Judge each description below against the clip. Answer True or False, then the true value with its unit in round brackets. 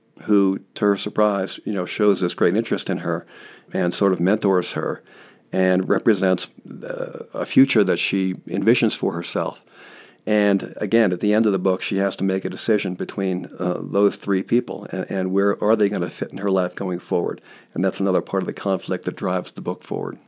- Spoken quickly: True (210 wpm)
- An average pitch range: False (1.7 semitones)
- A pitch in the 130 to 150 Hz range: False (95 Hz)